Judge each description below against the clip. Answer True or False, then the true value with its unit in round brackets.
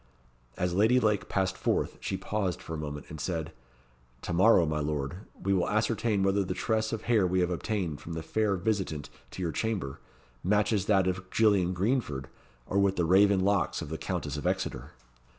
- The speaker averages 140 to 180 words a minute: False (195 wpm)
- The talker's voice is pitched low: True (95 Hz)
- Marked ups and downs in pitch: False (3.9 semitones)